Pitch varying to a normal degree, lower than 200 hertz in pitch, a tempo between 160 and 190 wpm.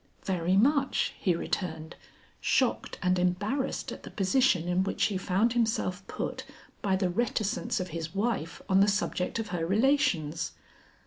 No: average, 4.1 semitones; high, 190 Hz; average, 150 wpm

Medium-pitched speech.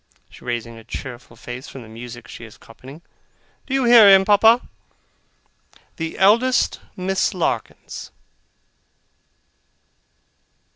Yes: medium, 160 Hz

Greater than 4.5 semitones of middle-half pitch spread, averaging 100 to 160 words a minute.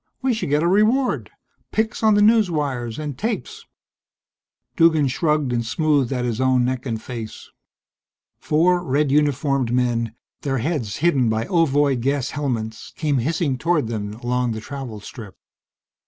Yes: average, 5.2 semitones; average, 150 wpm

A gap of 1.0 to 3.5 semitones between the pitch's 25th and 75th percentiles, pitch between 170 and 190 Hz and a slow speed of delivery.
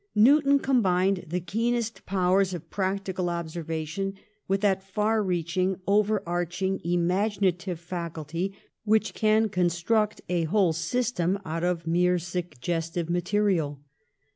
Yes: average, 3.2 semitones; medium, 185 Hz; slow, 115 wpm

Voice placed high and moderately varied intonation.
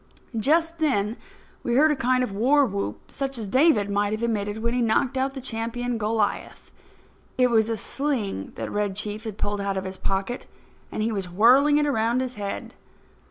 Yes: high, 230 Hz; average, 4.1 semitones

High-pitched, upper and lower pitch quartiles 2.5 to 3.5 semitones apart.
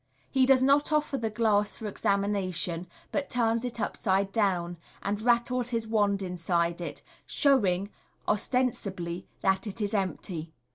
No: high, 205 Hz; average, 4.4 semitones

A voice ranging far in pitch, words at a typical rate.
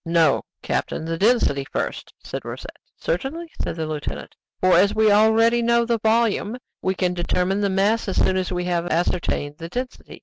No: average, 4.9 semitones; average, 180 wpm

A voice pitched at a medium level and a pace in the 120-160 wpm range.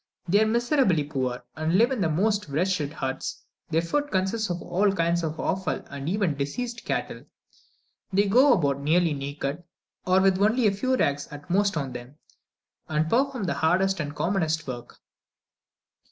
No: medium, 175 Hz; average, 170 wpm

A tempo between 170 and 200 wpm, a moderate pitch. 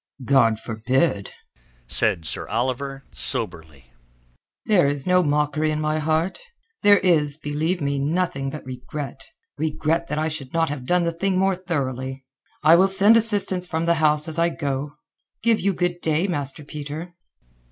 No: average, 155 wpm; medium, 155 Hz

